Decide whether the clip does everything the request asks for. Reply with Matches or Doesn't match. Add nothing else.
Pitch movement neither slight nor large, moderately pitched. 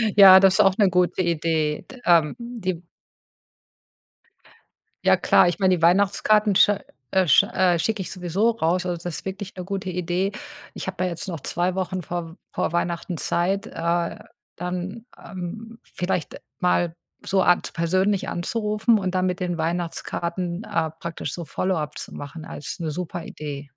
Doesn't match